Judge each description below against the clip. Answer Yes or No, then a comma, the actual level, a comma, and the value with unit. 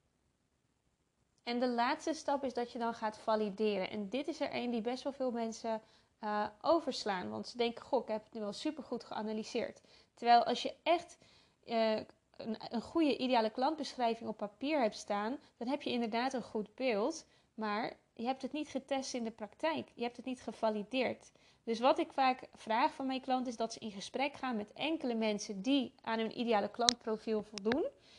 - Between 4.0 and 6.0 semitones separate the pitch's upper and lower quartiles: No, average, 3.4 semitones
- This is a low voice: No, high, 240 Hz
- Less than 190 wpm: No, average, 195 wpm